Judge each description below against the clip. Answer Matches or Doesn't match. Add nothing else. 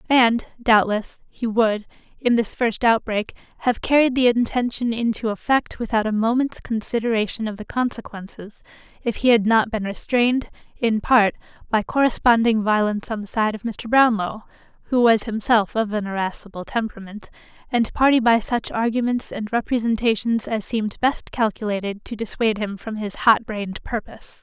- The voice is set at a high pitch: Matches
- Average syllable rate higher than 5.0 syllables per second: Matches